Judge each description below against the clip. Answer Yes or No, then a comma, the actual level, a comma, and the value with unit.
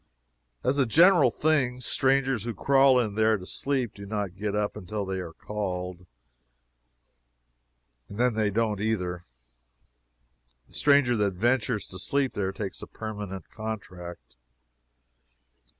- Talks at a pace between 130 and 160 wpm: Yes, slow, 135 wpm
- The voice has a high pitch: No, low, 110 Hz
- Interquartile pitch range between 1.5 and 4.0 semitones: No, average, 4.7 semitones